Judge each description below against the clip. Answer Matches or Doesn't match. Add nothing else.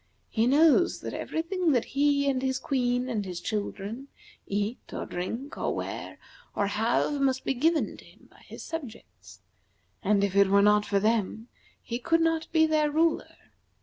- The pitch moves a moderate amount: Doesn't match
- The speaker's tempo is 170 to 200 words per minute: Matches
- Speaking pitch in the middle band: Doesn't match